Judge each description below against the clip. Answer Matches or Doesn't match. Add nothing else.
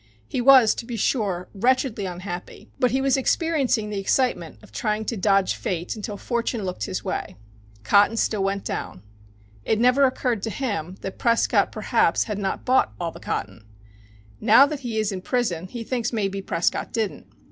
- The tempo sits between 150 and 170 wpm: Doesn't match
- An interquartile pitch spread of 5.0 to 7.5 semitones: Doesn't match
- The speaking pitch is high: Matches